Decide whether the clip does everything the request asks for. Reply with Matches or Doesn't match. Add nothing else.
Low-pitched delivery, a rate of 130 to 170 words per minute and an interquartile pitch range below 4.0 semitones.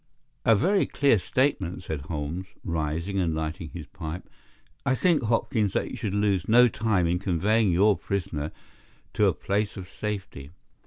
Doesn't match